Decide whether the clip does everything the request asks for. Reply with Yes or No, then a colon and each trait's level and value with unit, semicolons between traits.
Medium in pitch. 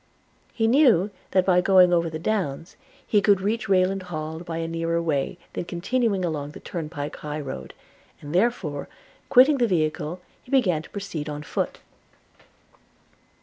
Yes: medium, 175 Hz